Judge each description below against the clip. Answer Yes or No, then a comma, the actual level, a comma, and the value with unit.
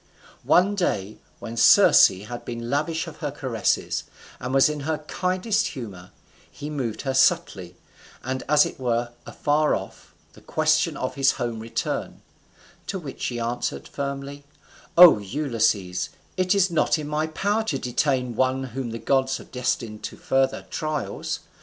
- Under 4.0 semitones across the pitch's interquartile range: No, average, 4.4 semitones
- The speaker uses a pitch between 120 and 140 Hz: Yes, low, 135 Hz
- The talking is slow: No, average, 155 wpm